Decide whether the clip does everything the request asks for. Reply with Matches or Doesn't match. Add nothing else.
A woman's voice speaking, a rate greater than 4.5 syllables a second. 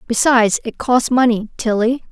Matches